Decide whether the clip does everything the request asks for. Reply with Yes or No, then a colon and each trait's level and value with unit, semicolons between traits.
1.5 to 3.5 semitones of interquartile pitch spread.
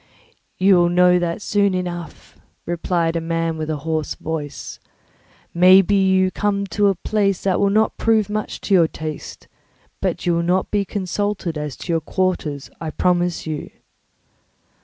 Yes: average, 3.1 semitones